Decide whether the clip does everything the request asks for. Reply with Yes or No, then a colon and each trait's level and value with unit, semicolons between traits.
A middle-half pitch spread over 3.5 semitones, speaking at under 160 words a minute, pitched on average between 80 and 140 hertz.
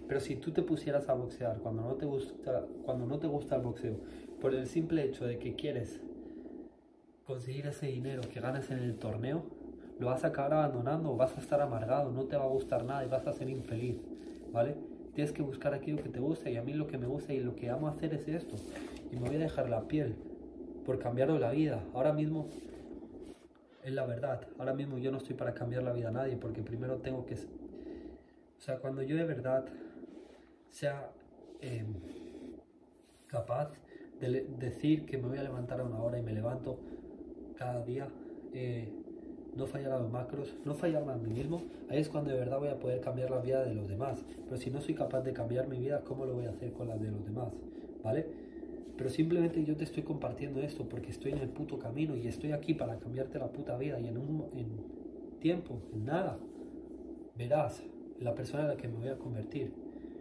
No: average, 4.0 semitones; fast, 215 wpm; low, 135 Hz